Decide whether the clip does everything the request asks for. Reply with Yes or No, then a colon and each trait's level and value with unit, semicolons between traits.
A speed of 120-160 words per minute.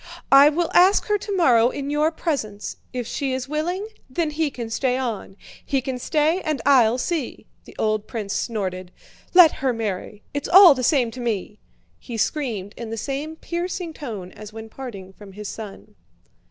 No: average, 180 wpm